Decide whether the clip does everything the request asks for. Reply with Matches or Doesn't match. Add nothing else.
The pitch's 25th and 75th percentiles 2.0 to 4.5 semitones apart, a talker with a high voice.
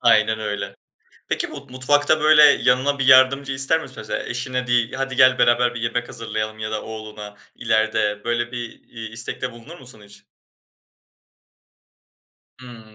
Doesn't match